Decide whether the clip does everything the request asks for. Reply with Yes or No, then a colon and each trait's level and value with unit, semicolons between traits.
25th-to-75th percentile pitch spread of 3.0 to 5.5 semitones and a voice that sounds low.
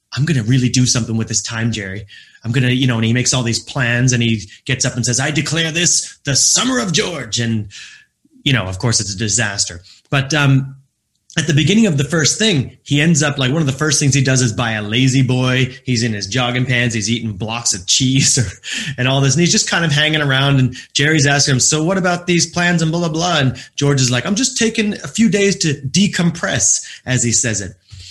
Yes: average, 4.9 semitones; low, 130 Hz